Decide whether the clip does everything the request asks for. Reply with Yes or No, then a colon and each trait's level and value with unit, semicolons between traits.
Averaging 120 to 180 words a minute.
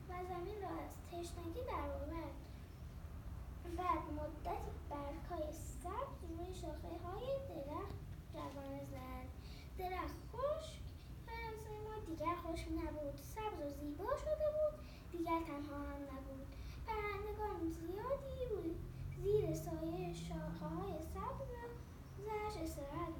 No: average, 110 wpm